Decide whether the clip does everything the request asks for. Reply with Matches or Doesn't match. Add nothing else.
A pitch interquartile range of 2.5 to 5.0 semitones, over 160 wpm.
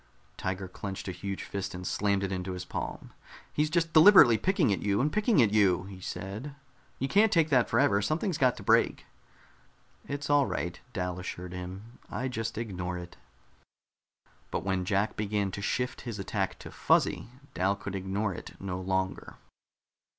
Doesn't match